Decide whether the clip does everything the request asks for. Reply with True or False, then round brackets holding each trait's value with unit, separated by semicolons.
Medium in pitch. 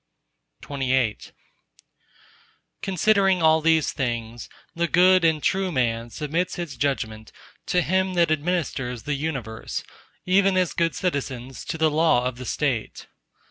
True (155 Hz)